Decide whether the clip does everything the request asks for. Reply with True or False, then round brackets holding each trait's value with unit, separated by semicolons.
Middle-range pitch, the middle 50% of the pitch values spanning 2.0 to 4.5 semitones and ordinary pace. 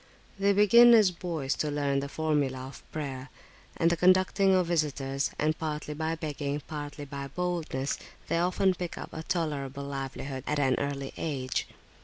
True (150 Hz; 3.8 semitones; 165 wpm)